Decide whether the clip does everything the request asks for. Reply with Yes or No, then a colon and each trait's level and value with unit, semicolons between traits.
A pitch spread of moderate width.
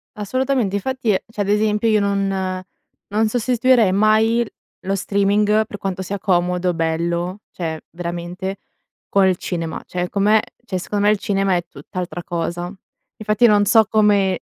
Yes: average, 3.0 semitones